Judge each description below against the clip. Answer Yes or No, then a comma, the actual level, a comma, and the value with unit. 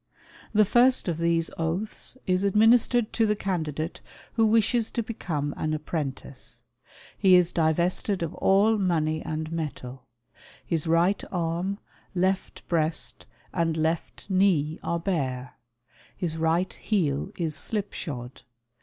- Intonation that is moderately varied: Yes, average, 4.1 semitones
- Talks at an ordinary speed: No, slow, 125 wpm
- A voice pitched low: No, medium, 170 Hz